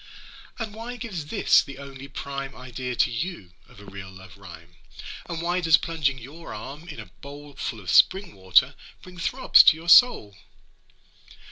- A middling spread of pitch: No, wide, 7.8 semitones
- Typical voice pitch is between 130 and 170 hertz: Yes, medium, 140 Hz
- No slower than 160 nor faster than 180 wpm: Yes, average, 170 wpm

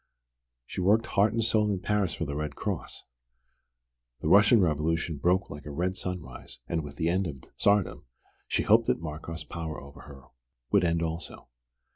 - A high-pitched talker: No, very low, 85 Hz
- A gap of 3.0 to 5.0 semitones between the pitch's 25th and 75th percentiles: Yes, average, 4.2 semitones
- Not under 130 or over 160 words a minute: No, average, 175 wpm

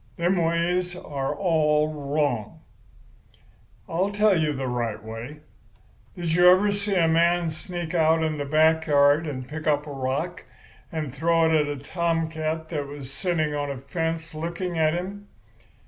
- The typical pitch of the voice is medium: Yes, medium, 160 Hz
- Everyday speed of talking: Yes, average, 160 wpm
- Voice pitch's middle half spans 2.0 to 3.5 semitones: Yes, average, 2.9 semitones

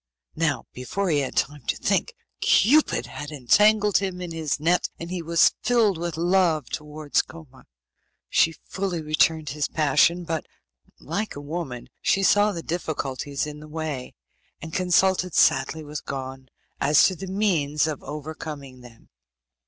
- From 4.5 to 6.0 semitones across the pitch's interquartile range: No, average, 3.6 semitones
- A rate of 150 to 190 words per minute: Yes, average, 155 wpm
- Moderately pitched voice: Yes, medium, 160 Hz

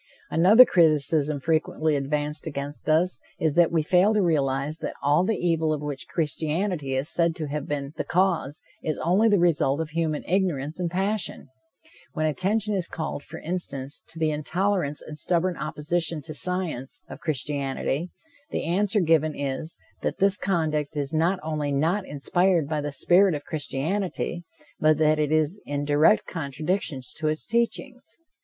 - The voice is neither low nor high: Yes, medium, 155 Hz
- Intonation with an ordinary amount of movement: Yes, average, 3.4 semitones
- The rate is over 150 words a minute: Yes, average, 165 wpm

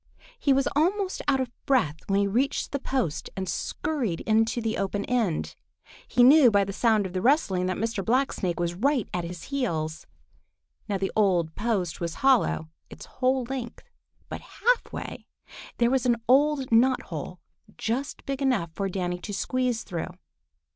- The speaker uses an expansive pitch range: Yes, wide, 6.0 semitones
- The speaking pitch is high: Yes, high, 225 Hz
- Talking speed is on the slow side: No, average, 170 wpm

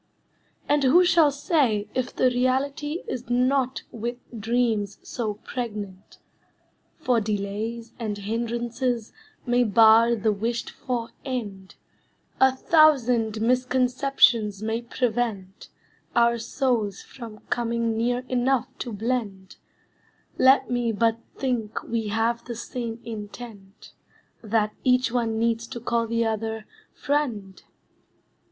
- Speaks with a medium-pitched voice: No, high, 235 Hz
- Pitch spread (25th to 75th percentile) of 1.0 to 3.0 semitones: Yes, narrow, 2.4 semitones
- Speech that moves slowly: Yes, slow, 115 wpm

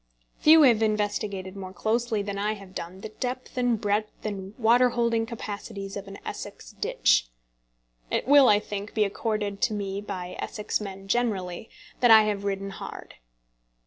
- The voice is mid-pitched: No, high, 210 Hz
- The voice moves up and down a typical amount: No, narrow, 2.3 semitones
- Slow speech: No, average, 165 wpm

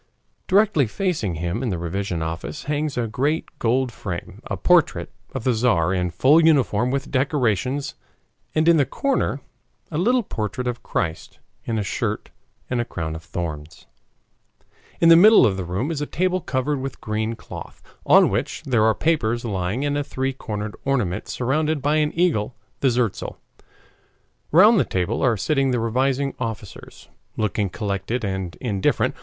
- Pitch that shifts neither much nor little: No, wide, 6.2 semitones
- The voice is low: Yes, low, 125 Hz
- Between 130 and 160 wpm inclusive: No, average, 170 wpm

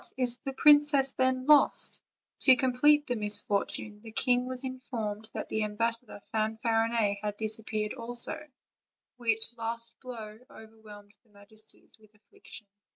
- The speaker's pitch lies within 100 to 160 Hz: No, high, 225 Hz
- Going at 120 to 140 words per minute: Yes, slow, 135 wpm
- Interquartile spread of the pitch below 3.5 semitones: Yes, average, 2.9 semitones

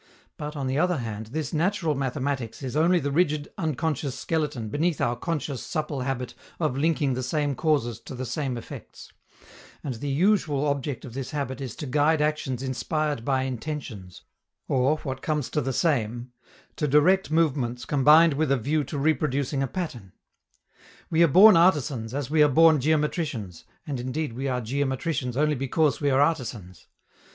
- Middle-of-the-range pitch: Yes, medium, 145 Hz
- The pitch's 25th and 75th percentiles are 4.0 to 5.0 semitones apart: No, average, 3.3 semitones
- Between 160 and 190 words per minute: Yes, average, 170 wpm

